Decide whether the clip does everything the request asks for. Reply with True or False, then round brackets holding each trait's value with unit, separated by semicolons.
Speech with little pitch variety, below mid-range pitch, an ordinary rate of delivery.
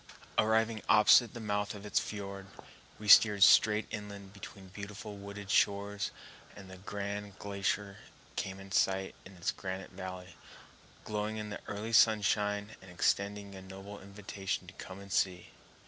True (1.3 semitones; 100 Hz; 150 wpm)